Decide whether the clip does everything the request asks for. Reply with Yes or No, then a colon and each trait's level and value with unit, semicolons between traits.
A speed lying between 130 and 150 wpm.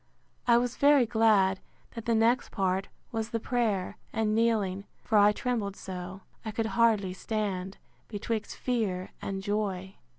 Yes: average, 145 wpm